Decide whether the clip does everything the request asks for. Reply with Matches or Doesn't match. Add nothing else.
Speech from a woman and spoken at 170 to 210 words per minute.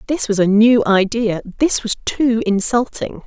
Doesn't match